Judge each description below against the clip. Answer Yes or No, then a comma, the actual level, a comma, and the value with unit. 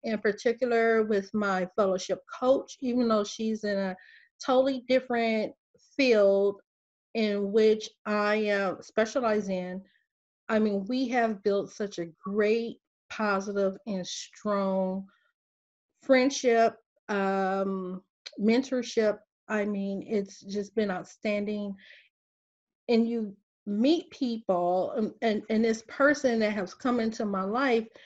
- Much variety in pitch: No, average, 2.8 semitones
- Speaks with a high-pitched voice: Yes, high, 215 Hz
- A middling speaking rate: No, slow, 120 wpm